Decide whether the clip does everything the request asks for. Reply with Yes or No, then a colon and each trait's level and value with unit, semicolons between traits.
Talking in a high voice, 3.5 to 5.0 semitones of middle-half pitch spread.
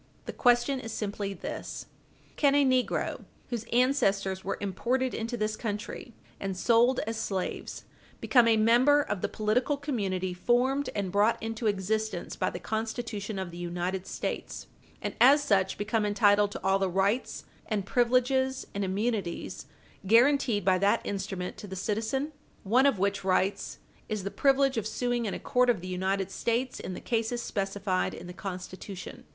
Yes: high, 215 Hz; average, 3.9 semitones